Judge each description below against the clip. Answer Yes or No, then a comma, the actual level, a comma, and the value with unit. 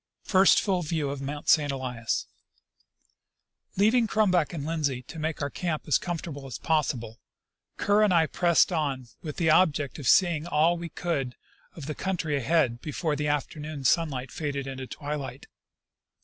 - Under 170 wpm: Yes, average, 160 wpm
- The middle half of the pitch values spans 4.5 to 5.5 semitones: No, average, 3.7 semitones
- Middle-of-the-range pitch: Yes, medium, 155 Hz